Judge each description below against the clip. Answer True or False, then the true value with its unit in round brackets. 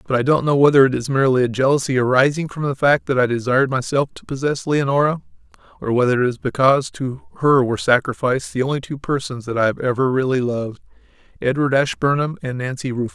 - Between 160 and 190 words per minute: False (200 wpm)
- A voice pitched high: False (130 Hz)